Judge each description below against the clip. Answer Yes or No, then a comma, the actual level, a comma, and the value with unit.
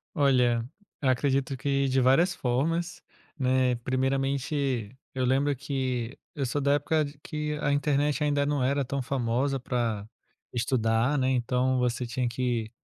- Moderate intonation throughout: No, narrow, 2.3 semitones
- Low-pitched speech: Yes, low, 130 Hz